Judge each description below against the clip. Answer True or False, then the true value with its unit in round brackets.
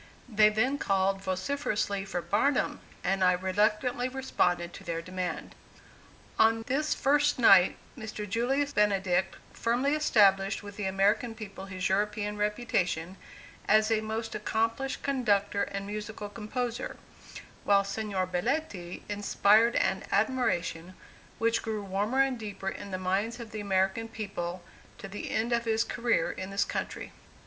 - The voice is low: False (210 Hz)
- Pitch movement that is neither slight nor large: True (3.0 semitones)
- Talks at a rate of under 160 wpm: True (140 wpm)